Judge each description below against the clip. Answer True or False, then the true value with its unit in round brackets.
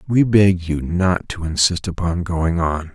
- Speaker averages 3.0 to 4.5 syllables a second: True (4.0 syllables/s)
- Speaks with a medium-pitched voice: False (90 Hz)